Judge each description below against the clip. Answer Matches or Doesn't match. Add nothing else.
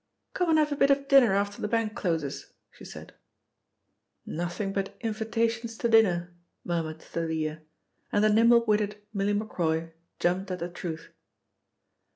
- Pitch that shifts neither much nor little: Matches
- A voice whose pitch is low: Doesn't match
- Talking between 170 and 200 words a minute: Doesn't match